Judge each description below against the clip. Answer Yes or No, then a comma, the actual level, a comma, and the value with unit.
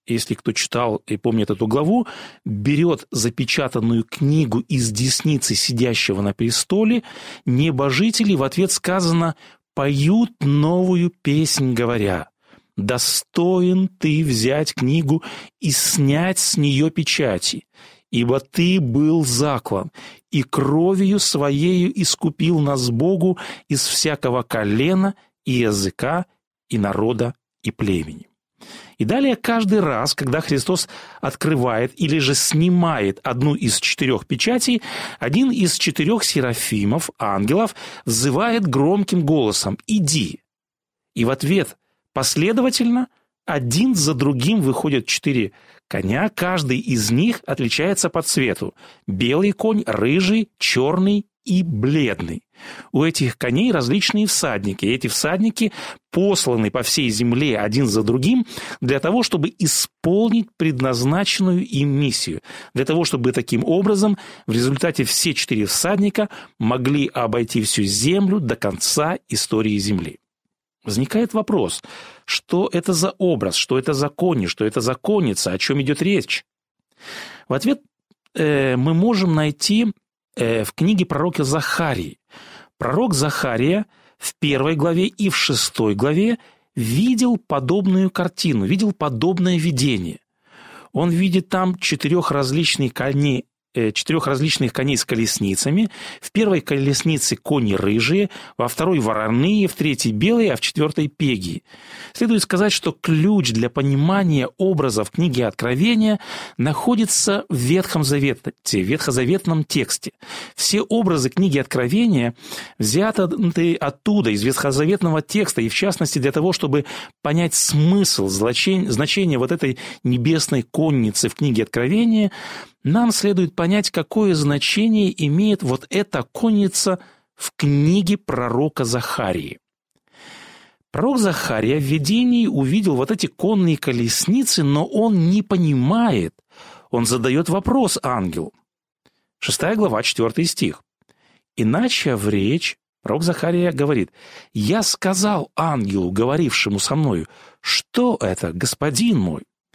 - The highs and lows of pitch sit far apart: Yes, wide, 6.9 semitones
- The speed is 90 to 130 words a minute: Yes, average, 120 wpm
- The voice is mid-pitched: Yes, medium, 155 Hz